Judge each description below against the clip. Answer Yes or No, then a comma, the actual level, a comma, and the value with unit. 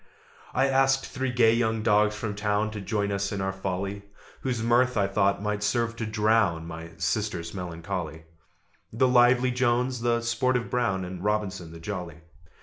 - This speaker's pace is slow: No, average, 165 wpm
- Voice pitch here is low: Yes, low, 105 Hz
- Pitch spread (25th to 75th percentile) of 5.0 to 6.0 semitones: No, average, 3.8 semitones